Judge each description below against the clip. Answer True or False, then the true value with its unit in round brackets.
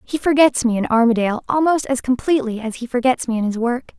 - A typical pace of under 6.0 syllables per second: False (6.2 syllables/s)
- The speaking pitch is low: False (250 Hz)